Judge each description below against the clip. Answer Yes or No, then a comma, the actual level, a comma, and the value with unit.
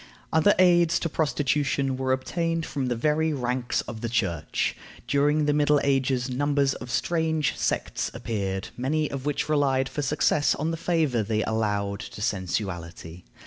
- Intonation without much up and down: No, average, 4.6 semitones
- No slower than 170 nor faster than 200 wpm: No, average, 155 wpm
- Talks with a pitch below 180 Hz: Yes, low, 135 Hz